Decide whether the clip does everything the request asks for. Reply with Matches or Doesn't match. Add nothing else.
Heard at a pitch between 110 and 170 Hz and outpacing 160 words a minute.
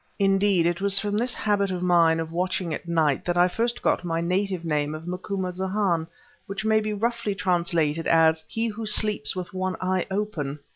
Doesn't match